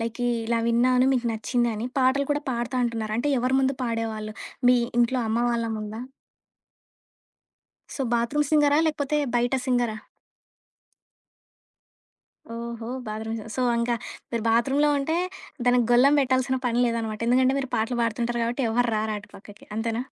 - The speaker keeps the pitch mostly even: Yes, narrow, 2.3 semitones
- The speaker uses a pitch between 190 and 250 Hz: Yes, high, 240 Hz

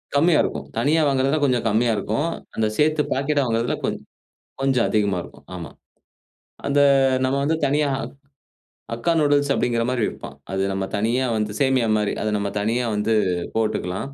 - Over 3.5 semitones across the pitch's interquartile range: Yes, average, 4.7 semitones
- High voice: No, low, 125 Hz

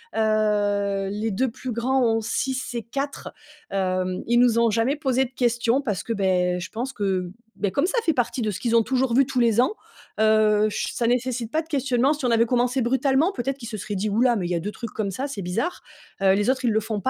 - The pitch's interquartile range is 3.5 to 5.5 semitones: Yes, average, 3.9 semitones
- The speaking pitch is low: No, high, 230 Hz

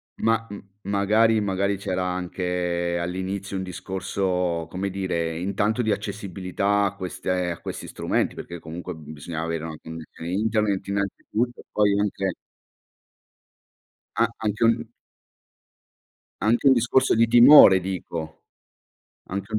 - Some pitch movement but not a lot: Yes, average, 3.0 semitones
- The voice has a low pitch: Yes, very low, 95 Hz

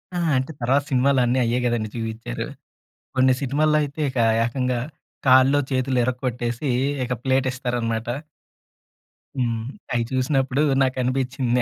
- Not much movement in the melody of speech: Yes, narrow, 1.6 semitones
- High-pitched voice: No, low, 130 Hz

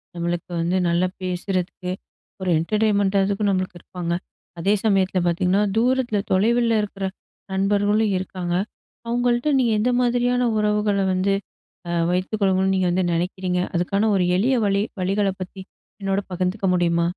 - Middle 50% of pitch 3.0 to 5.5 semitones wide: No, narrow, 2.5 semitones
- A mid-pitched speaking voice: No, high, 195 Hz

